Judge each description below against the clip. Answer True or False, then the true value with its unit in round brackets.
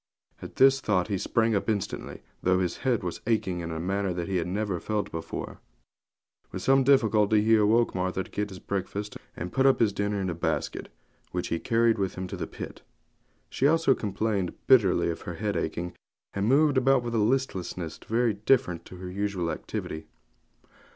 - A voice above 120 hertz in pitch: False (100 Hz)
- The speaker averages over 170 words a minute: True (190 wpm)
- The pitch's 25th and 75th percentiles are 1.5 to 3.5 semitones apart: False (4.1 semitones)